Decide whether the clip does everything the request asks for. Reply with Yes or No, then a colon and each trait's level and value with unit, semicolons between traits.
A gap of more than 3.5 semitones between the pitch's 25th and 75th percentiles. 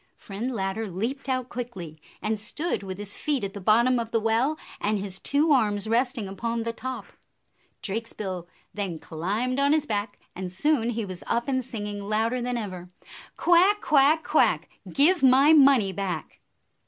Yes: average, 4.6 semitones